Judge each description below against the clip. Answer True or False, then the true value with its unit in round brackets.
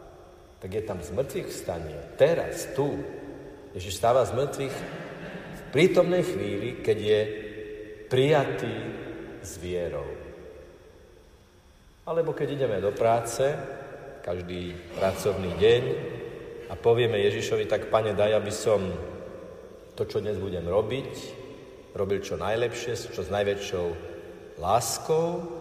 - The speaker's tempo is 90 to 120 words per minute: True (110 wpm)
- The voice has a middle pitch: True (170 Hz)